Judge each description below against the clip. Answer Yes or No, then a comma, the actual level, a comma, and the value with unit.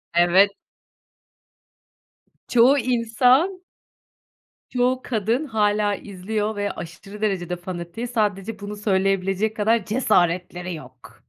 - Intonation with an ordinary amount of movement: Yes, average, 3.5 semitones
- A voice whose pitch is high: Yes, high, 210 Hz